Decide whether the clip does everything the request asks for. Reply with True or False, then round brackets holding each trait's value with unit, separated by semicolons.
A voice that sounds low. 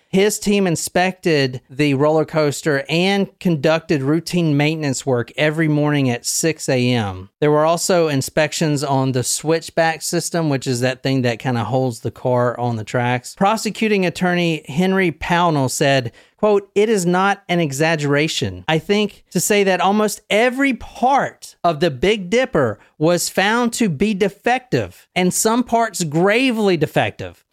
False (165 Hz)